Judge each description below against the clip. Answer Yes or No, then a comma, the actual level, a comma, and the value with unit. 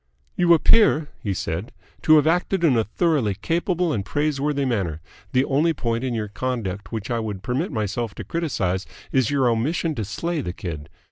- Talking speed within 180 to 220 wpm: Yes, average, 185 wpm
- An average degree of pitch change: No, wide, 7.0 semitones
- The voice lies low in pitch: Yes, low, 125 Hz